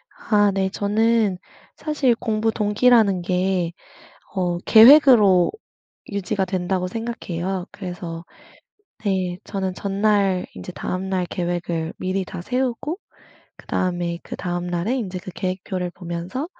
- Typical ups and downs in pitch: Yes, average, 3.3 semitones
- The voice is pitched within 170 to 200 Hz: Yes, high, 190 Hz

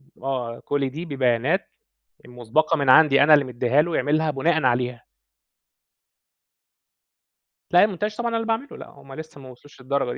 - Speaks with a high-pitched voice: No, medium, 140 Hz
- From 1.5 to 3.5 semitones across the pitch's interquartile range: No, average, 4.0 semitones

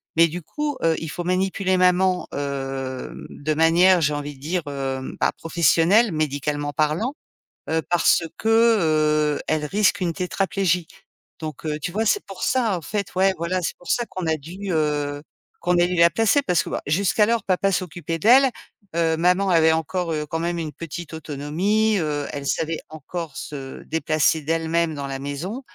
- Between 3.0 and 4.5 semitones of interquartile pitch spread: Yes, average, 3.6 semitones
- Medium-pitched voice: Yes, medium, 165 Hz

